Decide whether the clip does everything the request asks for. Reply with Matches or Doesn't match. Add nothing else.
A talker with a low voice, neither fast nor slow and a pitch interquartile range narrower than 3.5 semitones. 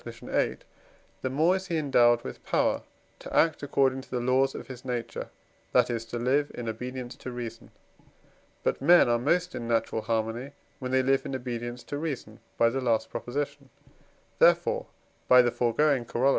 Matches